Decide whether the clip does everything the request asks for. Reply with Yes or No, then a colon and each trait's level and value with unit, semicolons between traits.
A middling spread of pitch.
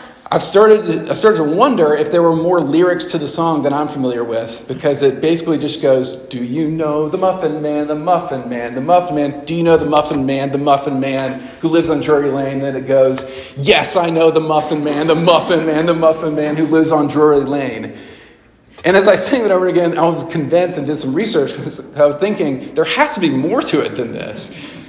Yes: average, 3.0 semitones